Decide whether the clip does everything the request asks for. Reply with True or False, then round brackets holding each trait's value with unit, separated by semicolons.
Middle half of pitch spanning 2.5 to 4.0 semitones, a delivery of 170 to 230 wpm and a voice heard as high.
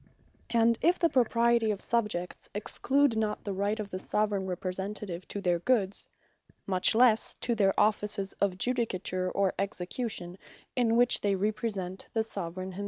False (3.5 semitones; 155 wpm; 205 Hz)